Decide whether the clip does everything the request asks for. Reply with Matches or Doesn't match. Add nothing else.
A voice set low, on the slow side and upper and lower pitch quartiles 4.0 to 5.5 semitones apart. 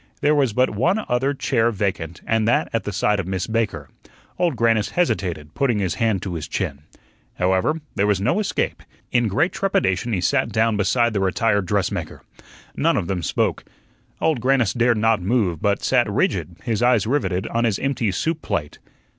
Doesn't match